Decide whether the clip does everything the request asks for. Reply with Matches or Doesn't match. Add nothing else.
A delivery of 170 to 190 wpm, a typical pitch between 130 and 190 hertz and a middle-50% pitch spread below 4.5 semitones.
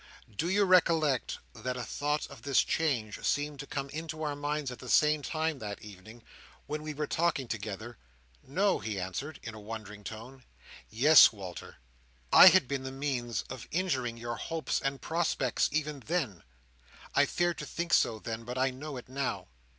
Doesn't match